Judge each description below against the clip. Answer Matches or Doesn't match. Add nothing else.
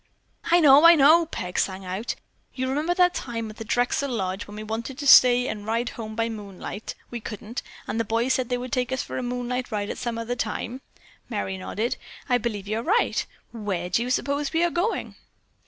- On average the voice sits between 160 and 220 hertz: Doesn't match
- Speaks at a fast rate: Matches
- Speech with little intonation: Doesn't match